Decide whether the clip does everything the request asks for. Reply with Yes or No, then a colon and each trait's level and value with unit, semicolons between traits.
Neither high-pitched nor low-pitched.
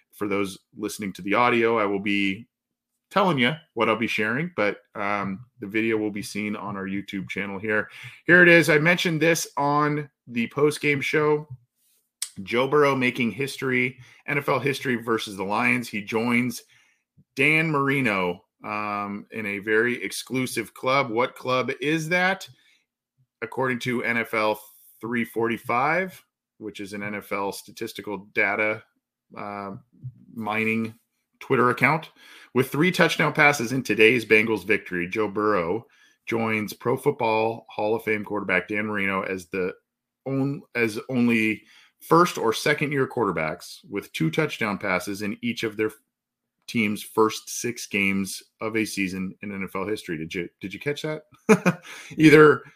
No: low, 115 Hz